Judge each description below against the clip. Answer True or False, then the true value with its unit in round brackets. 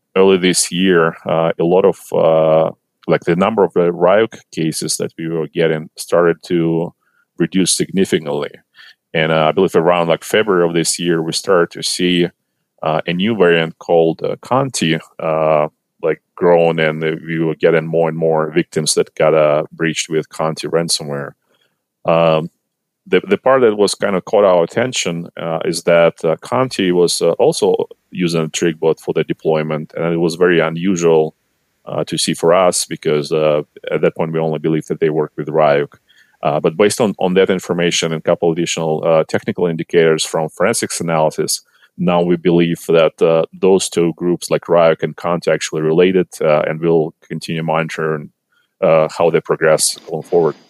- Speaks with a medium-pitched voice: False (80 Hz)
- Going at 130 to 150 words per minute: False (180 wpm)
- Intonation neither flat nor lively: False (1.6 semitones)